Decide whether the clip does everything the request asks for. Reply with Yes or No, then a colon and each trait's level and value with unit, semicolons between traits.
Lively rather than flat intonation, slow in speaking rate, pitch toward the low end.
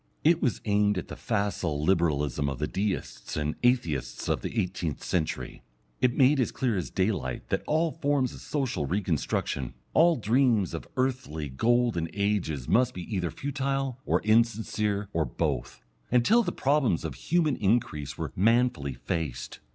No: wide, 8.0 semitones; average, 155 wpm; low, 105 Hz